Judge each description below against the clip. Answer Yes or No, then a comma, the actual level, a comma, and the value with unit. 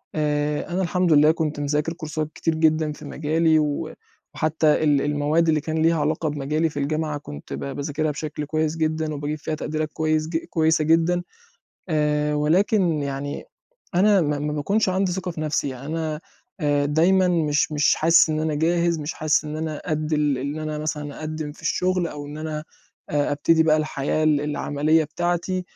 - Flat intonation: Yes, narrow, 1.6 semitones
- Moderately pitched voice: Yes, medium, 155 Hz